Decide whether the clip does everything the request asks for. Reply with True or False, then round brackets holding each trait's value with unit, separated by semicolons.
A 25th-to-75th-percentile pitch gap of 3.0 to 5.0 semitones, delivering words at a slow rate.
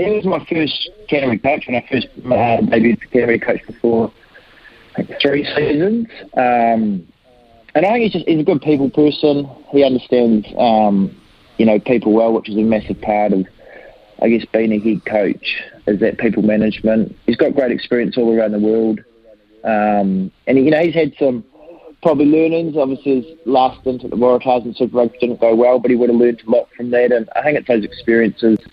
False (4.1 semitones; 200 wpm)